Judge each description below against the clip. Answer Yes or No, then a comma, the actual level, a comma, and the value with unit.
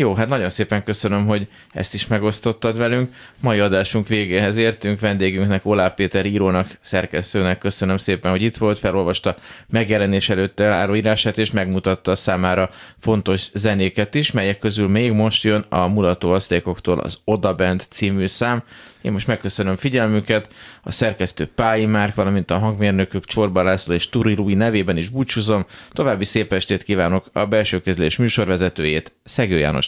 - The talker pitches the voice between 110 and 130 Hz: No, low, 100 Hz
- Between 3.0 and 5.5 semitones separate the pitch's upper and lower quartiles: No, narrow, 2.5 semitones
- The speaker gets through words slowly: No, average, 150 wpm